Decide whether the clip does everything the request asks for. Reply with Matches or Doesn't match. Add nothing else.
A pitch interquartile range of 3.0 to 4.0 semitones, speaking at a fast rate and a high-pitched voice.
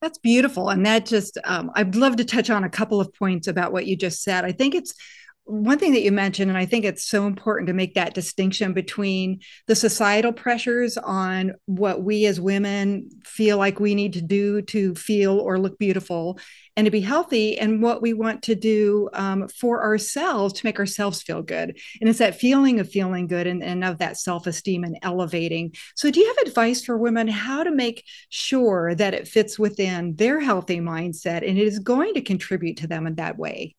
Matches